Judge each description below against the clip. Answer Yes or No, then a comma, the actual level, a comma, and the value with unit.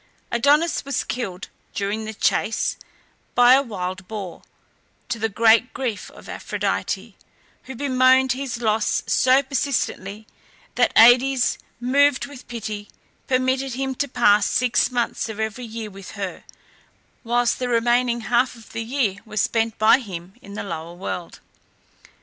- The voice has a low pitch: No, high, 235 Hz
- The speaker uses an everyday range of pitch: Yes, average, 3.4 semitones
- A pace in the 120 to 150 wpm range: Yes, average, 145 wpm